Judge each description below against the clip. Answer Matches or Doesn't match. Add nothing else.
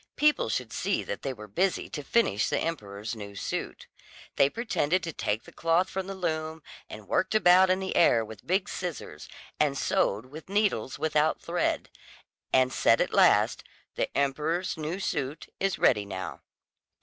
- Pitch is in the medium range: Matches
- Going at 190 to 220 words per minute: Doesn't match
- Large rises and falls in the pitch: Matches